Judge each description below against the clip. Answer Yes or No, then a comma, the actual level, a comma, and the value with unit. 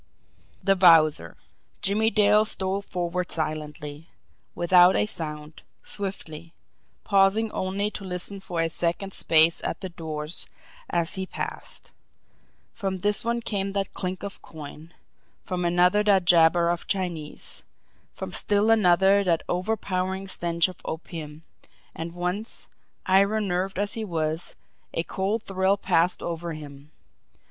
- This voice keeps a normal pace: No, slow, 130 wpm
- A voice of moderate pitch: Yes, medium, 180 Hz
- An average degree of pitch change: Yes, average, 3.1 semitones